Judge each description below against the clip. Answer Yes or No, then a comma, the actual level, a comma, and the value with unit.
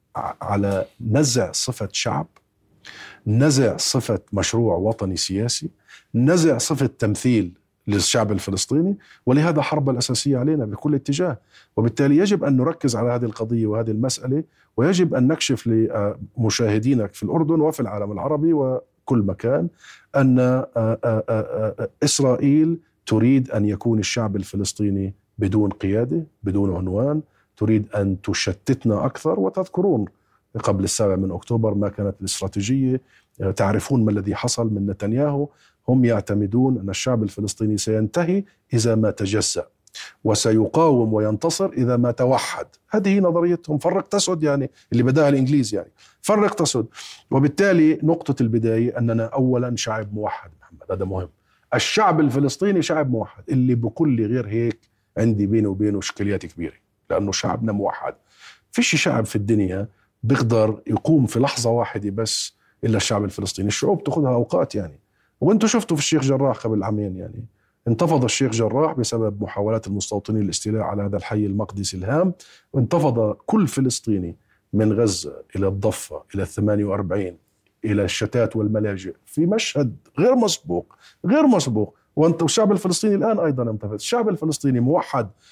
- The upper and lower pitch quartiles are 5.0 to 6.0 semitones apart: Yes, wide, 5.5 semitones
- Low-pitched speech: Yes, low, 115 Hz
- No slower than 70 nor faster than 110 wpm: No, average, 130 wpm